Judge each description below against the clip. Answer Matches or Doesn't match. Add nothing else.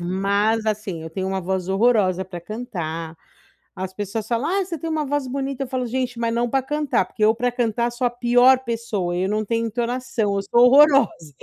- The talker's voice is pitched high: Matches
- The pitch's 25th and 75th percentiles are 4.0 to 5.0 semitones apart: Matches